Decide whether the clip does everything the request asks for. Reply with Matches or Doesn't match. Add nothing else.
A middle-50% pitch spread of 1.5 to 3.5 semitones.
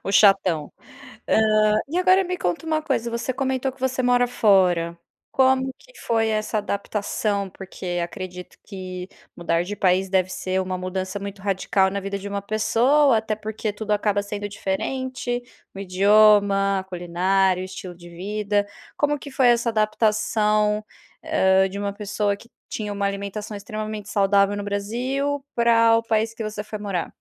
Matches